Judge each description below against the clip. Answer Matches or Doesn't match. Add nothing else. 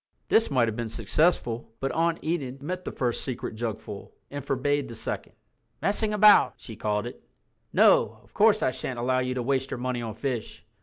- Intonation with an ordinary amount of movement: Matches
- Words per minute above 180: Matches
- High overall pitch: Doesn't match